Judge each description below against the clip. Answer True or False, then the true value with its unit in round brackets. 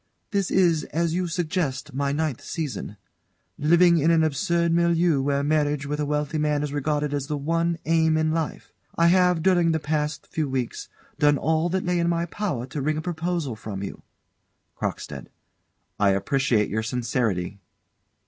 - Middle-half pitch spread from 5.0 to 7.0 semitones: False (3.3 semitones)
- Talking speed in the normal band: True (170 wpm)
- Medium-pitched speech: True (155 Hz)